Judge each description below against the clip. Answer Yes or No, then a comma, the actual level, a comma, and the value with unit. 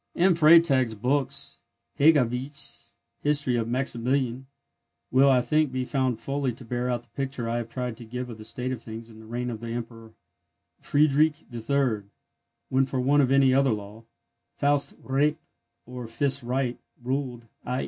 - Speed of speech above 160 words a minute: Yes, average, 170 wpm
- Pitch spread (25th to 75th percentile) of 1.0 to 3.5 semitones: Yes, average, 2.8 semitones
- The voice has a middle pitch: No, low, 125 Hz